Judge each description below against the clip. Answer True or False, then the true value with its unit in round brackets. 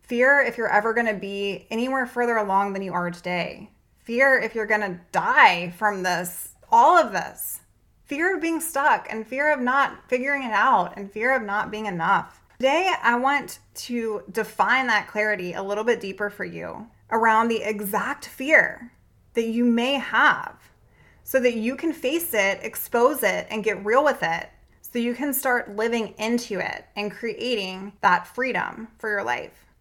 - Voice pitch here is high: True (225 Hz)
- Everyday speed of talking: True (175 wpm)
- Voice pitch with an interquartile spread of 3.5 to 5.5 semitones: True (3.8 semitones)